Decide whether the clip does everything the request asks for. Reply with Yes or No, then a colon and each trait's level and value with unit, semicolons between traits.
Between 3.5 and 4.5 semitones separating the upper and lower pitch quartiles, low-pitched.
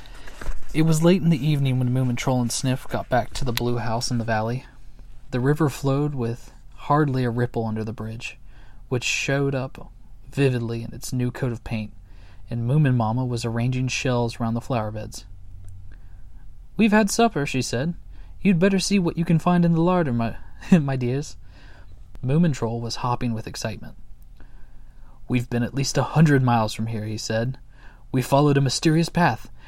Yes: average, 3.9 semitones; low, 120 Hz